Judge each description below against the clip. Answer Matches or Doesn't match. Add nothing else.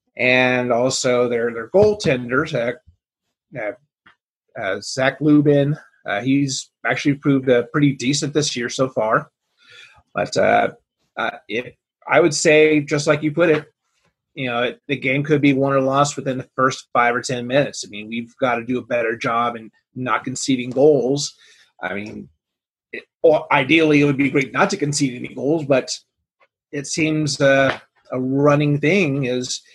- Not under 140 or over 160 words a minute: Doesn't match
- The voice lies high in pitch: Doesn't match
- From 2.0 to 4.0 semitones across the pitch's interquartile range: Matches